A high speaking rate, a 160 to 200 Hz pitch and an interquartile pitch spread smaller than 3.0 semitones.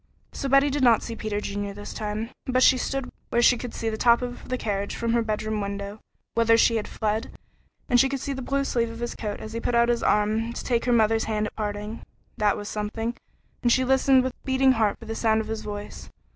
No: fast, 245 wpm; high, 230 Hz; narrow, 2.6 semitones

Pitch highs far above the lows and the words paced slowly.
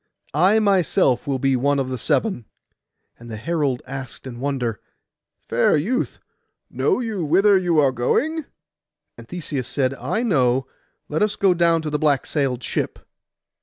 No: wide, 6.0 semitones; average, 160 wpm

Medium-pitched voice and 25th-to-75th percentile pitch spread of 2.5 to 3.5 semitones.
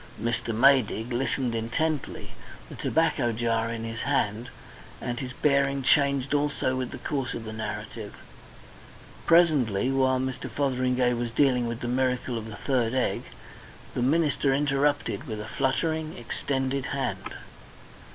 No: low, 130 Hz; average, 3.0 semitones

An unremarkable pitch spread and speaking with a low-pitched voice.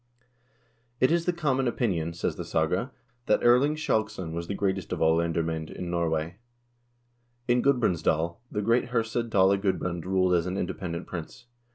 No: wide, 6.1 semitones; very low, 95 Hz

